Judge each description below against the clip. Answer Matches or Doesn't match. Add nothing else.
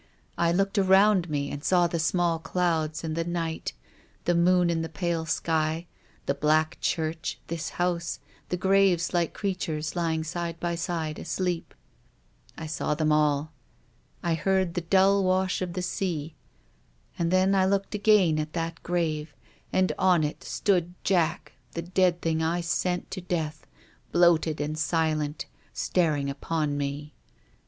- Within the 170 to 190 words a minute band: Doesn't match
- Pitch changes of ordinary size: Doesn't match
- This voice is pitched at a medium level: Matches